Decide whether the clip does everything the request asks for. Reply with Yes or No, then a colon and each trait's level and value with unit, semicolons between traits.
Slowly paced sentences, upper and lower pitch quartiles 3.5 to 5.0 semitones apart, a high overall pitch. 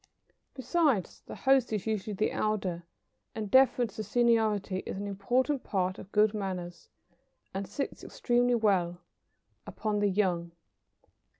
Yes: slow, 130 wpm; average, 4.0 semitones; high, 210 Hz